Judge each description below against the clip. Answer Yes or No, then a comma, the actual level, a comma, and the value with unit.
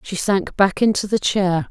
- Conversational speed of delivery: No, fast, 210 wpm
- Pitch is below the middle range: No, high, 190 Hz